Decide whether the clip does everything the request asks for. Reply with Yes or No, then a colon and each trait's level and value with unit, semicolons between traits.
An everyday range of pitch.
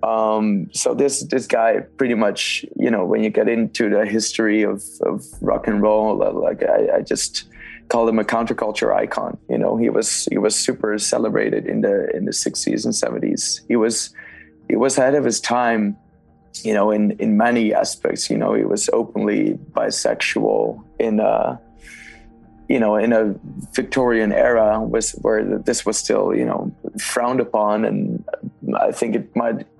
No: narrow, 1.5 semitones